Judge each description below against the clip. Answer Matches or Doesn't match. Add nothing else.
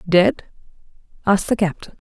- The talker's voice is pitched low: Doesn't match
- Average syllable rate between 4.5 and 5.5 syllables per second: Doesn't match